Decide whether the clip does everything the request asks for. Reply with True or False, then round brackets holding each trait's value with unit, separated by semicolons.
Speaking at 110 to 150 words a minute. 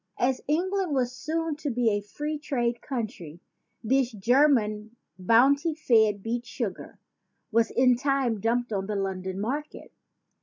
True (145 wpm)